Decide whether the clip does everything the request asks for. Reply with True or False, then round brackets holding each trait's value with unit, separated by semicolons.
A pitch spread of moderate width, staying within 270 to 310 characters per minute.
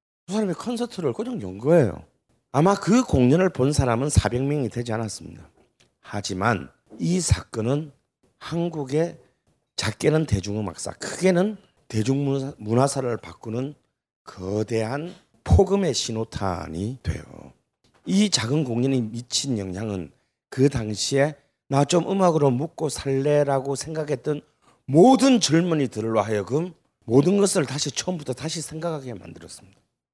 False (6.2 semitones; 285 characters per minute)